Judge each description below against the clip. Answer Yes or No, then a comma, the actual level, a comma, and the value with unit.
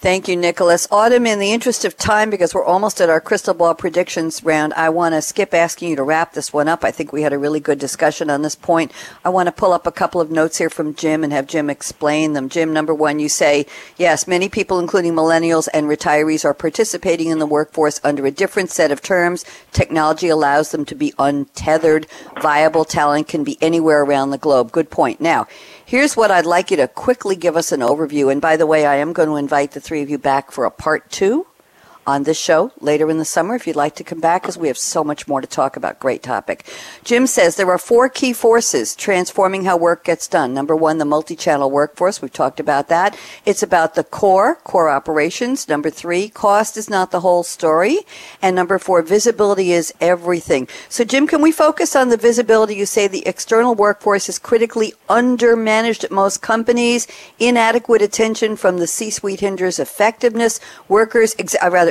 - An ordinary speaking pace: No, fast, 215 wpm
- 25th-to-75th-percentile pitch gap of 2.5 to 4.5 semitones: No, average, 5.1 semitones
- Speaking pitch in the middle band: Yes, medium, 175 Hz